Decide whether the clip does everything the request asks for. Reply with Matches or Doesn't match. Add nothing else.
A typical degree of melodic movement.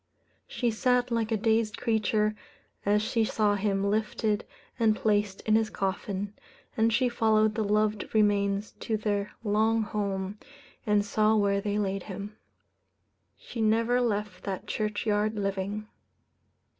Doesn't match